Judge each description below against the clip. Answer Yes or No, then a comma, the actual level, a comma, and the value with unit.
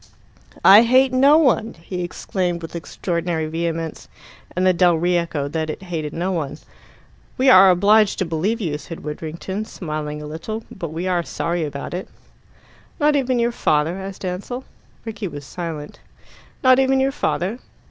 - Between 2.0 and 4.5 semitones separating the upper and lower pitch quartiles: No, average, 5.0 semitones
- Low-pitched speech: No, medium, 180 Hz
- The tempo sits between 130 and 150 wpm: No, average, 165 wpm